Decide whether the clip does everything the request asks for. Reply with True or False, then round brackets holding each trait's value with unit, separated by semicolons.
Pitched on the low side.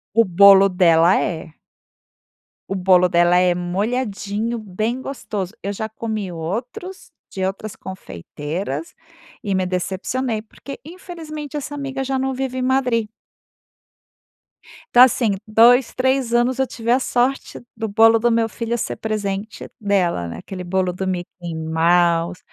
False (210 Hz)